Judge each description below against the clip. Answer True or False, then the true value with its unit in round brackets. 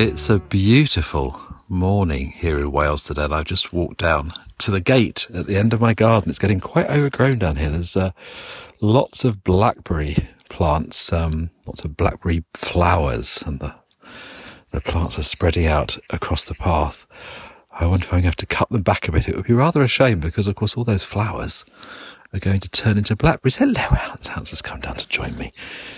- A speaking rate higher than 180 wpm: True (205 wpm)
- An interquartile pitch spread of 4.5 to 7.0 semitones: True (5.0 semitones)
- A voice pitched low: True (95 Hz)